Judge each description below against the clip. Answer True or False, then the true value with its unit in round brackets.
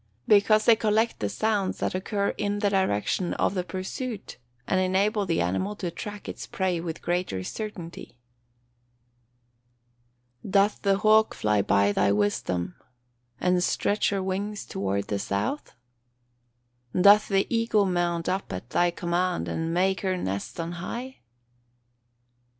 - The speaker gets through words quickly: False (145 wpm)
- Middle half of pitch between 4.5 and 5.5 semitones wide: False (3.7 semitones)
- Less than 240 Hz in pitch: True (185 Hz)